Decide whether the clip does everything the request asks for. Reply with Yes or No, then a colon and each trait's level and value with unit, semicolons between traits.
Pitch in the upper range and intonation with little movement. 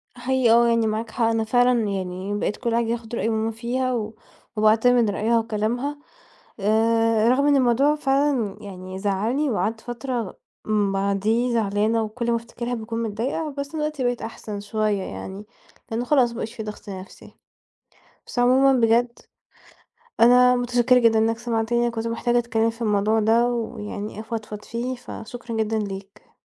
Yes: high, 230 Hz; narrow, 2.2 semitones